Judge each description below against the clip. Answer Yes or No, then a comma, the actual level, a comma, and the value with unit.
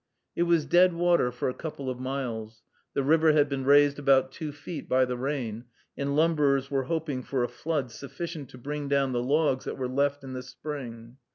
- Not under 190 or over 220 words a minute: Yes, average, 200 wpm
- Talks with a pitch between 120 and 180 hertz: Yes, medium, 140 Hz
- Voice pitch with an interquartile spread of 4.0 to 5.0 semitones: No, average, 2.8 semitones